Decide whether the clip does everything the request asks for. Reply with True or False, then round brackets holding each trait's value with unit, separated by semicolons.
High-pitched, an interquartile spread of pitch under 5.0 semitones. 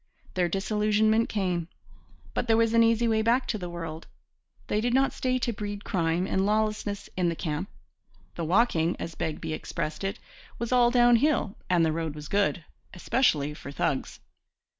False (200 Hz; 5.4 semitones)